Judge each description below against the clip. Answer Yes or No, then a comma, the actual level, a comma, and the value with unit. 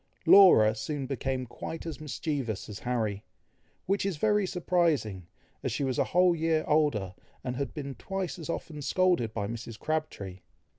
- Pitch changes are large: Yes, wide, 6.6 semitones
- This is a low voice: No, medium, 145 Hz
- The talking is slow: No, average, 160 wpm